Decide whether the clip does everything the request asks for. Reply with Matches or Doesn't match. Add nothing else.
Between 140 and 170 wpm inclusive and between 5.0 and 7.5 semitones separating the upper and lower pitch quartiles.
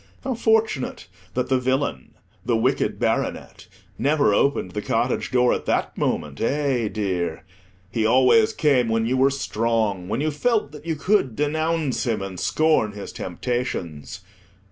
Matches